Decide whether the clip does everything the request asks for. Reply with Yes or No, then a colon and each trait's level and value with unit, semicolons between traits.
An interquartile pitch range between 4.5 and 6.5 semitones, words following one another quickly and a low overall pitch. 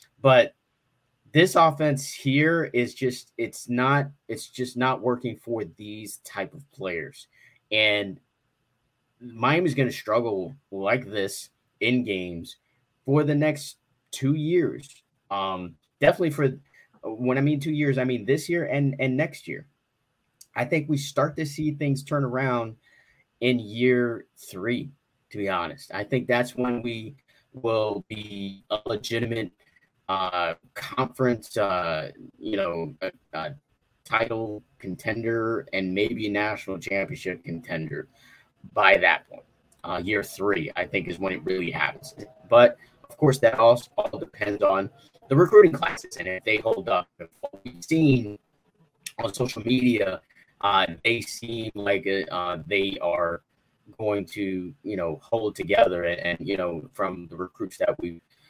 No: average, 5.0 semitones; average, 145 wpm; low, 125 Hz